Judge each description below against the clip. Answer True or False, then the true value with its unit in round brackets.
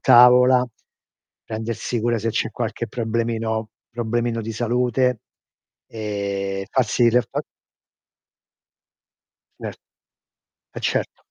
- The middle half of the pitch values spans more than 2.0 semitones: False (1.6 semitones)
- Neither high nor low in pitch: False (115 Hz)